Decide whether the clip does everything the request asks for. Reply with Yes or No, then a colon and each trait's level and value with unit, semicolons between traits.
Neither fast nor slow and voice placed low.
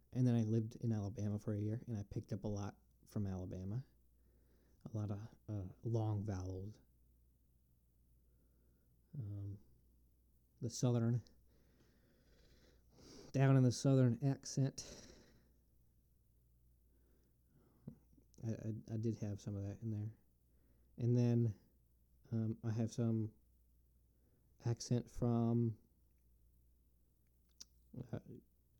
No: slow, 105 wpm; low, 100 Hz